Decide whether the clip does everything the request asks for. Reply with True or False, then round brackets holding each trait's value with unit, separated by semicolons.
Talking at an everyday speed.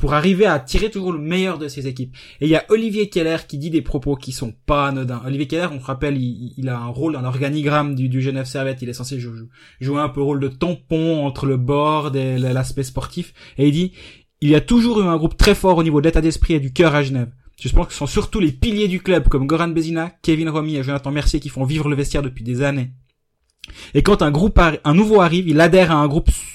False (265 wpm)